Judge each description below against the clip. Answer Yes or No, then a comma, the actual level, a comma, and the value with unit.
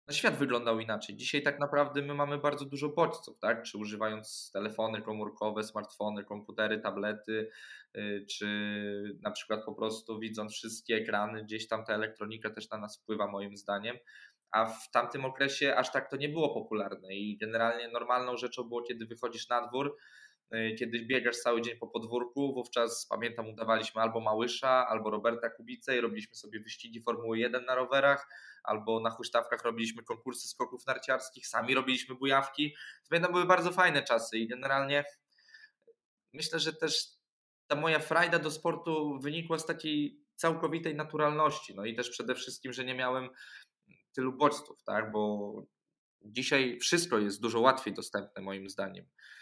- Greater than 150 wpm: Yes, fast, 160 wpm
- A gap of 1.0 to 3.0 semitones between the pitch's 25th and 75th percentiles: No, average, 4.6 semitones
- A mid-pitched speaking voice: No, low, 120 Hz